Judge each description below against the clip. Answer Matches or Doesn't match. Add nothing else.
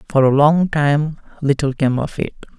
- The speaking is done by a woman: Doesn't match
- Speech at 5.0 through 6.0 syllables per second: Doesn't match